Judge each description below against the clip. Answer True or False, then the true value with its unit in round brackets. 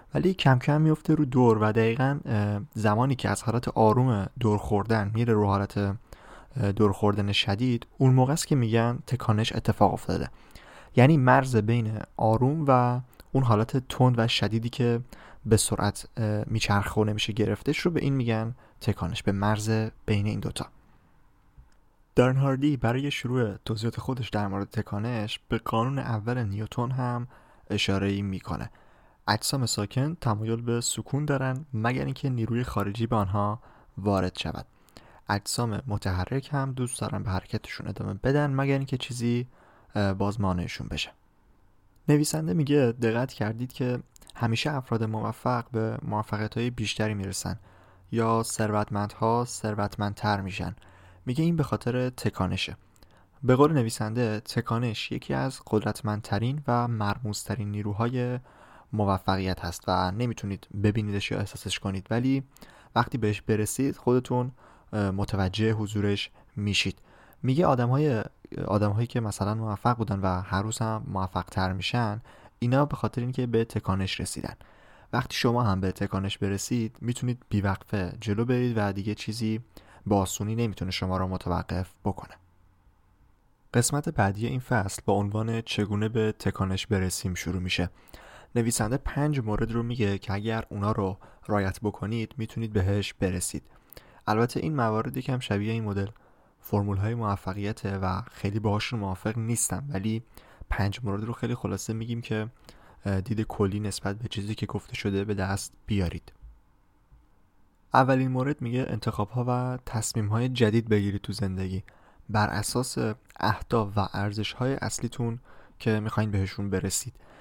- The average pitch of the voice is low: True (110 Hz)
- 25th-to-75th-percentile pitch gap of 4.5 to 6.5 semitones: False (3.4 semitones)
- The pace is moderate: True (140 wpm)